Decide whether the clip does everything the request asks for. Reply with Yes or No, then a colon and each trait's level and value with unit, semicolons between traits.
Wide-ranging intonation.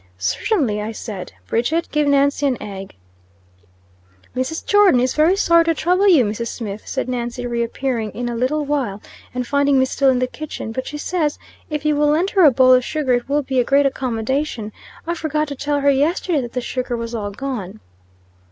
No: average, 4.0 semitones